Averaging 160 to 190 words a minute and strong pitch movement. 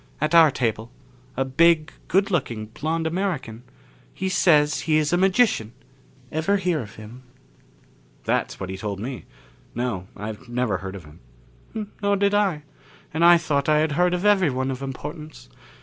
Yes: average, 165 wpm; wide, 6.5 semitones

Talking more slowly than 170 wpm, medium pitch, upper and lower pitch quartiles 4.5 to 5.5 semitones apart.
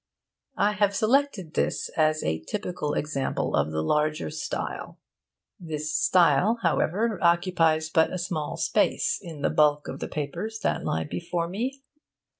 Yes: average, 145 wpm; medium, 165 Hz; average, 5.0 semitones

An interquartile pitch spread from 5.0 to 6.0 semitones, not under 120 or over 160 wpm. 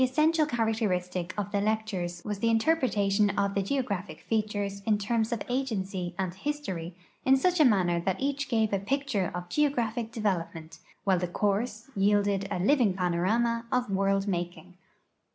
No: average, 4.0 semitones; average, 155 wpm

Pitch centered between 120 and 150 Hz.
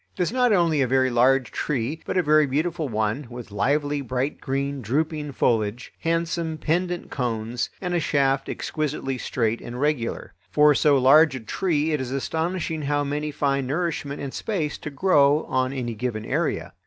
Yes: medium, 140 Hz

